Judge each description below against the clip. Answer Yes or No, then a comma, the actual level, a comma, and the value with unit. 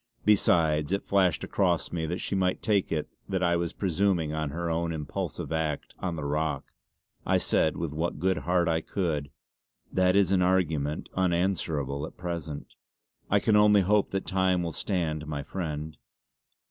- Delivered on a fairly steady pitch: No, average, 3.2 semitones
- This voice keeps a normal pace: Yes, average, 170 wpm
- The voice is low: Yes, very low, 85 Hz